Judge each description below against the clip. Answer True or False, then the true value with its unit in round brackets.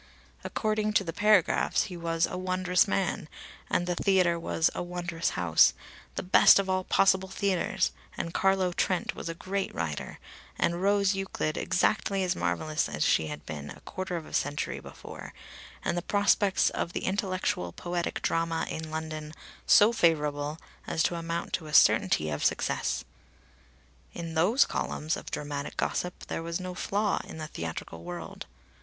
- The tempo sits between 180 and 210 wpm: False (165 wpm)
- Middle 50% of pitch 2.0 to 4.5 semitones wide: True (3.3 semitones)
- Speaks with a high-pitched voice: False (175 Hz)